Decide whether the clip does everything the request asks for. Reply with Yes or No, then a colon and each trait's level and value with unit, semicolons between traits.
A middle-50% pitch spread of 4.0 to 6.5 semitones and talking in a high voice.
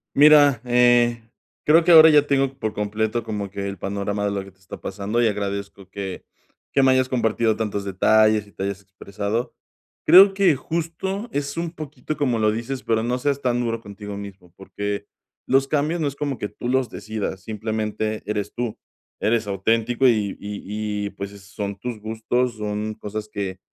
No: average, 4.3 semitones; low, 110 Hz